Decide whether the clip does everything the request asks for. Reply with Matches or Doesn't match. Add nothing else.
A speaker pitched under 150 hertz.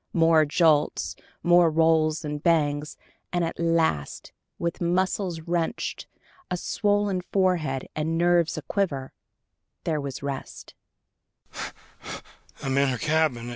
Doesn't match